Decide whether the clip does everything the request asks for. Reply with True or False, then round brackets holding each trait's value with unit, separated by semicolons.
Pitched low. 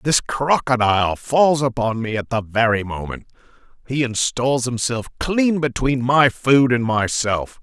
True (125 Hz)